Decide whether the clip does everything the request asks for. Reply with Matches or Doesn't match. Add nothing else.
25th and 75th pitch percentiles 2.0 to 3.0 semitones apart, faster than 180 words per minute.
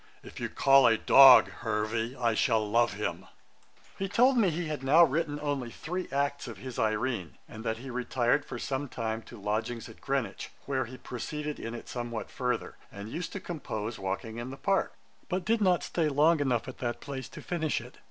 Doesn't match